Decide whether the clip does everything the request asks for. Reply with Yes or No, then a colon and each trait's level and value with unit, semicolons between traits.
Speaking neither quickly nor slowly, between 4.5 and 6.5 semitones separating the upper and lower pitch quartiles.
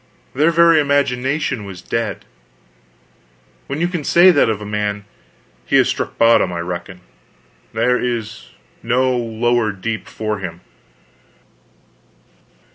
No: slow, 120 wpm; average, 5.1 semitones